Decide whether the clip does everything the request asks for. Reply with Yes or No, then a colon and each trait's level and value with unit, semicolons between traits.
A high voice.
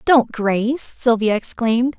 Yes: high, 240 Hz